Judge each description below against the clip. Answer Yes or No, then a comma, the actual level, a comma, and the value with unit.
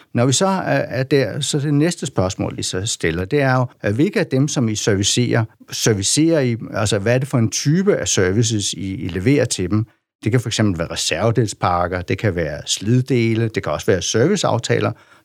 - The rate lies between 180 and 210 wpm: Yes, average, 200 wpm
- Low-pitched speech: Yes, low, 120 Hz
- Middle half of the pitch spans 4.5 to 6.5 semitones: Yes, average, 5.0 semitones